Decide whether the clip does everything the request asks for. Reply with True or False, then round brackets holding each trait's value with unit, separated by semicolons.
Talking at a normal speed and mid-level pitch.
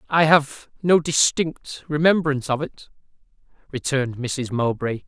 False (120 wpm; 145 Hz)